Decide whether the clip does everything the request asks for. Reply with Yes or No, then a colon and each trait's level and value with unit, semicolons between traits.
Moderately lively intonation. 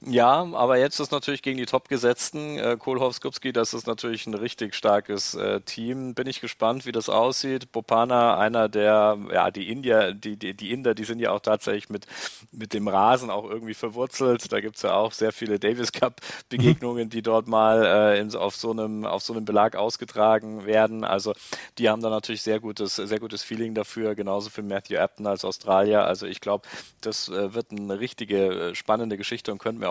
No: narrow, 2.1 semitones